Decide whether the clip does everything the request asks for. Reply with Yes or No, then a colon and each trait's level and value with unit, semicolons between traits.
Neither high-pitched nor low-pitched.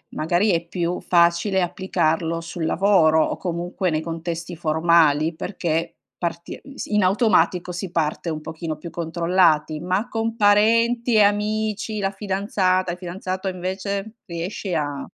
Yes: medium, 180 Hz